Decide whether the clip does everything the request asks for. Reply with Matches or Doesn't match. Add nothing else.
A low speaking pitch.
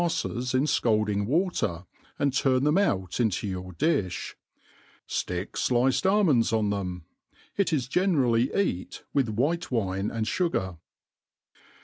Matches